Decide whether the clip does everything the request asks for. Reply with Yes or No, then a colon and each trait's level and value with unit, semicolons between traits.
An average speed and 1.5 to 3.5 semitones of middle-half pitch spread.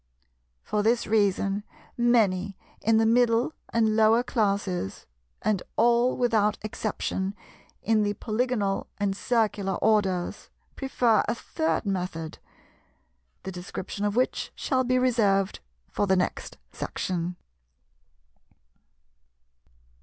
No: slow, 105 wpm; average, 3.1 semitones